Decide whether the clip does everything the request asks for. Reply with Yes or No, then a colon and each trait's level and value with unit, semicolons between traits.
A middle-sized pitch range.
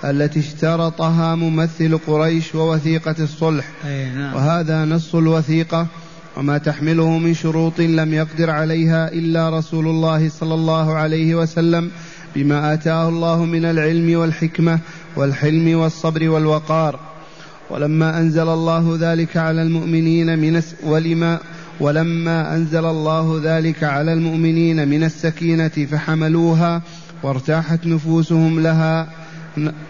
No: narrow, 0.8 semitones